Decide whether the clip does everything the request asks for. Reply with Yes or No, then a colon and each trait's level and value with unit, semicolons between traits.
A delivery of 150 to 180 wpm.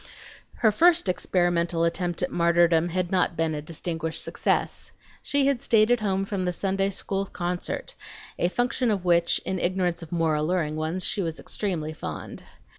Yes: average, 170 wpm